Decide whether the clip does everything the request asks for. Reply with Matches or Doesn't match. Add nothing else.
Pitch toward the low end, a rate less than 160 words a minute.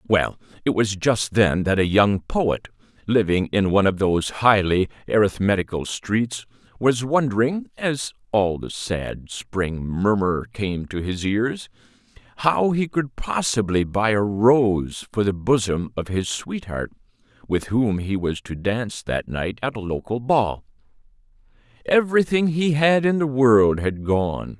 Matches